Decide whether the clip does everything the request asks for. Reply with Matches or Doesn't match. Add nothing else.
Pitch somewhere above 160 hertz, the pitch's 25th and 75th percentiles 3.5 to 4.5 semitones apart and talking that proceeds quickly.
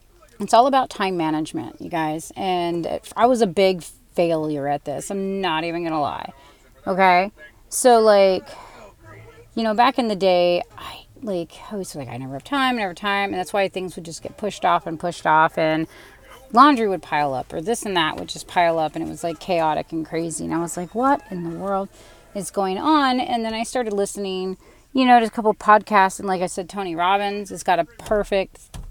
Matches